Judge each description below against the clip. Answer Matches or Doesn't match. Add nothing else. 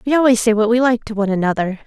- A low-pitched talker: Doesn't match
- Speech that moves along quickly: Matches